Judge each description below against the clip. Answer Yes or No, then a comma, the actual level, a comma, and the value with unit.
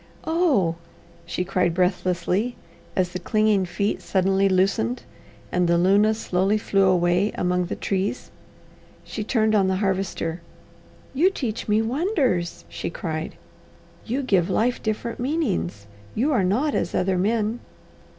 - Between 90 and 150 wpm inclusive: Yes, slow, 135 wpm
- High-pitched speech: Yes, high, 195 Hz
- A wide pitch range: No, average, 3.8 semitones